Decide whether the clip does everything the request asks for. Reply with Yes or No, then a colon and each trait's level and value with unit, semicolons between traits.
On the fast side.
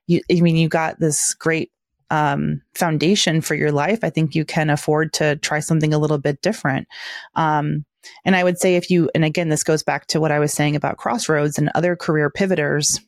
Yes: fast, 215 wpm